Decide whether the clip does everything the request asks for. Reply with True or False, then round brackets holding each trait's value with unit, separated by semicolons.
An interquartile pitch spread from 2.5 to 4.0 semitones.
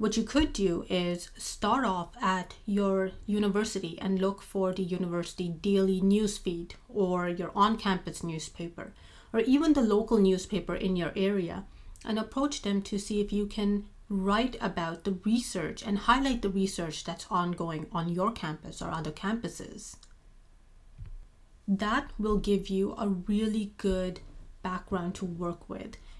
True (2.8 semitones)